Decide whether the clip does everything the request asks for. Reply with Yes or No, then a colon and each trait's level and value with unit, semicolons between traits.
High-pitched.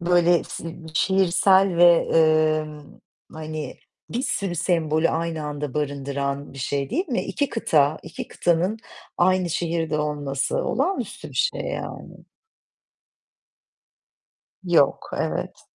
No: medium, 165 Hz